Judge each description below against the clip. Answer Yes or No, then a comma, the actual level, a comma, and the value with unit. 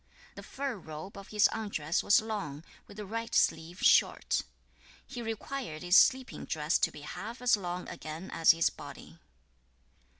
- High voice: Yes, high, 195 Hz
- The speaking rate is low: No, average, 170 wpm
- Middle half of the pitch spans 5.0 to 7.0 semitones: Yes, wide, 5.6 semitones